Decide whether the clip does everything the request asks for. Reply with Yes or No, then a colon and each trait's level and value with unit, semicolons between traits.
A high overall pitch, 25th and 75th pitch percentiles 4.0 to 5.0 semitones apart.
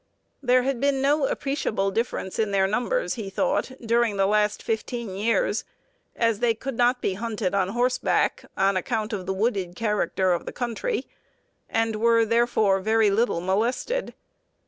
No: high, 225 Hz; average, 3.6 semitones